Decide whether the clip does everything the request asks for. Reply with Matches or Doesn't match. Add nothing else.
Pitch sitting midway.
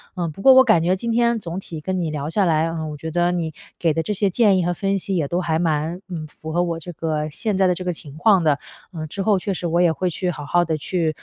Matches